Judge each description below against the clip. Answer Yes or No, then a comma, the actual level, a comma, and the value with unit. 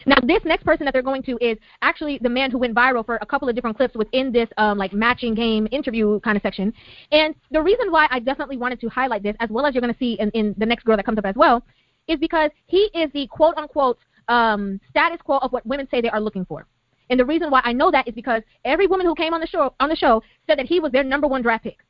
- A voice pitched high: Yes, very high, 255 Hz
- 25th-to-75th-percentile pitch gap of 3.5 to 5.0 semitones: Yes, average, 4.7 semitones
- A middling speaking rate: No, fast, 285 wpm